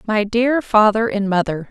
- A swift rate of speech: No, average, 175 wpm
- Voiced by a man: No, female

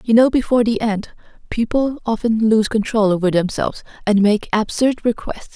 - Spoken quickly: No, average, 160 wpm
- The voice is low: No, high, 220 Hz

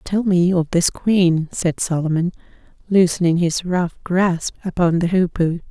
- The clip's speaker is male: No, female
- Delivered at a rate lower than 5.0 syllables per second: Yes, 4.2 syllables/s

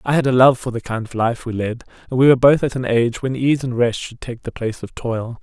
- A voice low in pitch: Yes, low, 125 Hz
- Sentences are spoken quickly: Yes, fast, 310 wpm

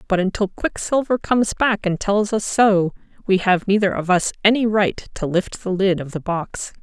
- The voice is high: Yes, high, 200 Hz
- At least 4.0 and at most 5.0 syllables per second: Yes, 4.7 syllables/s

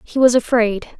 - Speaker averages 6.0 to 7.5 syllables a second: No, 4.5 syllables/s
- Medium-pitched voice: No, high, 230 Hz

